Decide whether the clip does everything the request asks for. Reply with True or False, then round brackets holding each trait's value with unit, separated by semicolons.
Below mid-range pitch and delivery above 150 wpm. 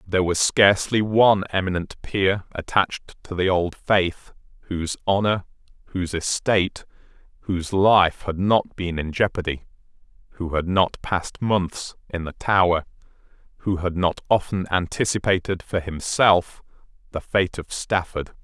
False (90 Hz; 135 wpm)